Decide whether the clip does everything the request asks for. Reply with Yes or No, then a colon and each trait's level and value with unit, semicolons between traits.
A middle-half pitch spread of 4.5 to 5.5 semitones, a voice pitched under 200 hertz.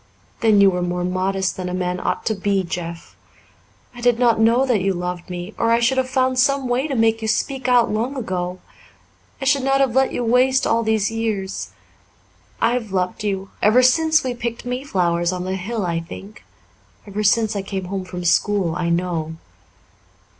No: average, 5.2 semitones; high, 210 Hz